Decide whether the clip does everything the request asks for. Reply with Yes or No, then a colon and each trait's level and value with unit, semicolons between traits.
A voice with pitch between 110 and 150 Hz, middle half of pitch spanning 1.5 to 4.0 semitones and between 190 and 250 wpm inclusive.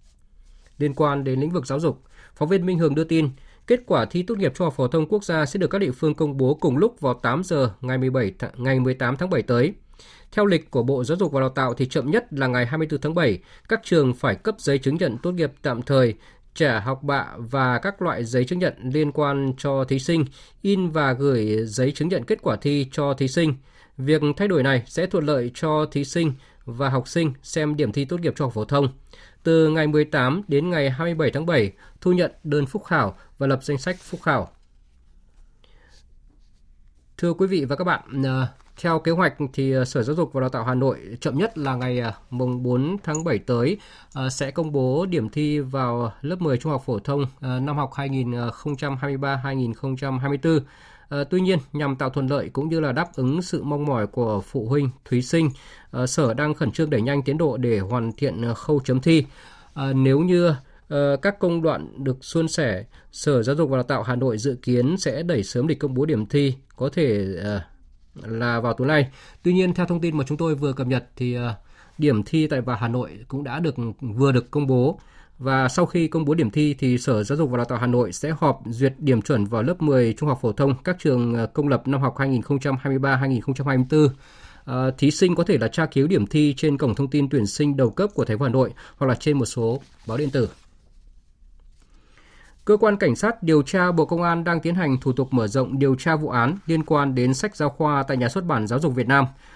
Yes: medium, 140 Hz; average, 3.7 semitones; average, 225 wpm